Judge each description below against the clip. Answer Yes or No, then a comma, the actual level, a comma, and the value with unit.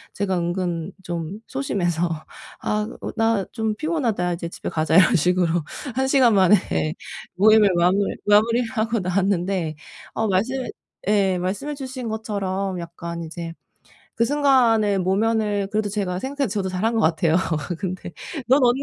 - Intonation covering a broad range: No, average, 4.1 semitones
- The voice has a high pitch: Yes, high, 200 Hz